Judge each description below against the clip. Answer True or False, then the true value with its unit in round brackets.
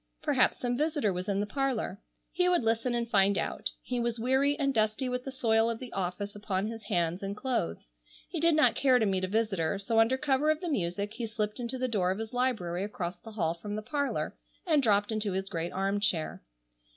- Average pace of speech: False (225 wpm)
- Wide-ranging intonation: False (4.6 semitones)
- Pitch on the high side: True (220 Hz)